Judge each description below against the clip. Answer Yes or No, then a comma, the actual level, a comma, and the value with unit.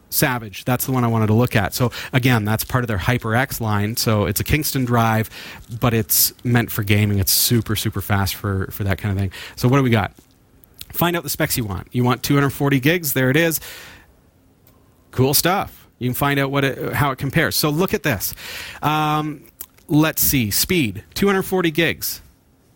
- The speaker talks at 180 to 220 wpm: Yes, average, 200 wpm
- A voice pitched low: Yes, low, 125 Hz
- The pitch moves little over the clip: No, average, 5.1 semitones